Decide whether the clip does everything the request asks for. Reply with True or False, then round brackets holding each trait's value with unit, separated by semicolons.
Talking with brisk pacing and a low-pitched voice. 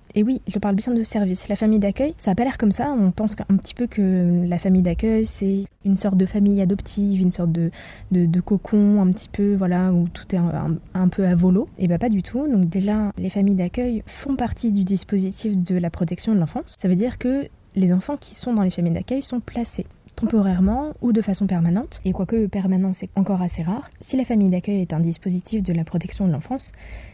False (235 wpm; 195 Hz)